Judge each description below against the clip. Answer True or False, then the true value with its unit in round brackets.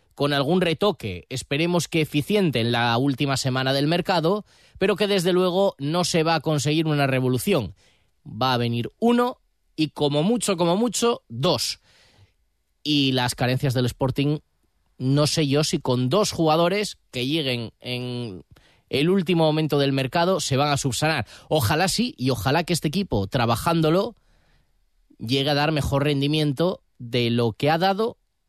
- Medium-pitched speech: True (145 Hz)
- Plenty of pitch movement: True (5.8 semitones)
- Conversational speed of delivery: True (160 wpm)